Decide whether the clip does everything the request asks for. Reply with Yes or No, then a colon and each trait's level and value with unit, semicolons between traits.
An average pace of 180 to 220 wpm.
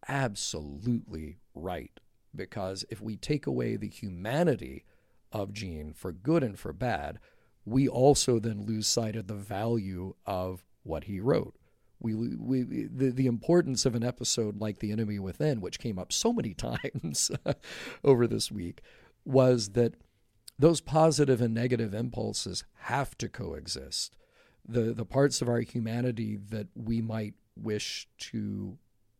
No: average, 145 wpm